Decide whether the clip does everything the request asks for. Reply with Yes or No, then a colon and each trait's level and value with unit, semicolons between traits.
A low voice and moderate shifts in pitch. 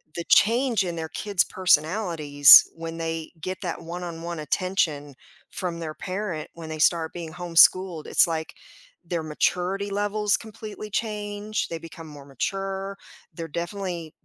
No: medium, 175 Hz; average, 3.4 semitones